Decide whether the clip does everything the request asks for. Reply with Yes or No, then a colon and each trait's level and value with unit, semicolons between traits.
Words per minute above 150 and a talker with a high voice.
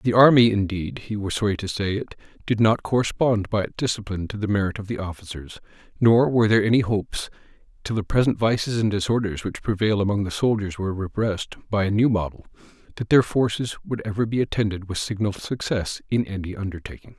No: average, 195 wpm; low, 105 Hz